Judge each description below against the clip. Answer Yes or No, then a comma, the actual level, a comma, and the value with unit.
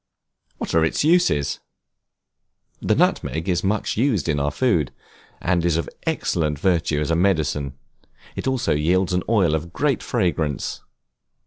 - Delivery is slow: No, average, 145 wpm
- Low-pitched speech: Yes, very low, 85 Hz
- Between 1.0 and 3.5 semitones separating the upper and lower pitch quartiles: No, average, 4.0 semitones